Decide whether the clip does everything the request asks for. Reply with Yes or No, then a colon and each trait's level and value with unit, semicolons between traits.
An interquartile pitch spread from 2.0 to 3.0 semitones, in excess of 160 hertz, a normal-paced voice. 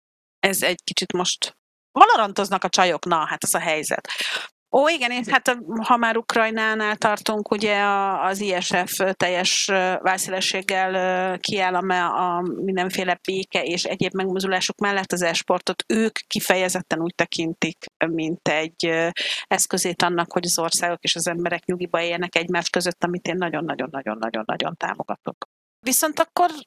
Yes: narrow, 2.4 semitones; medium, 185 Hz; average, 135 wpm